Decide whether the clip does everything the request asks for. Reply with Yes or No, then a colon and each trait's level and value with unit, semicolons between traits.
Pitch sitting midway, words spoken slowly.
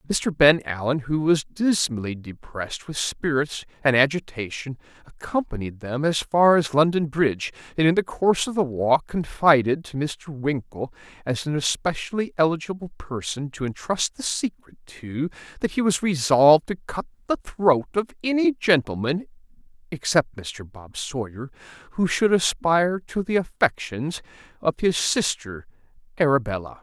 No: medium, 150 Hz; average, 145 wpm